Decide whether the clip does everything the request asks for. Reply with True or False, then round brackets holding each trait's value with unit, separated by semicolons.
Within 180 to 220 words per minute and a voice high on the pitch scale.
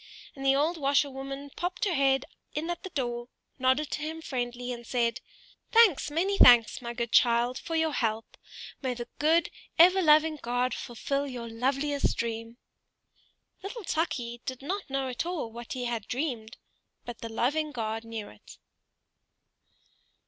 False (155 wpm; 265 Hz)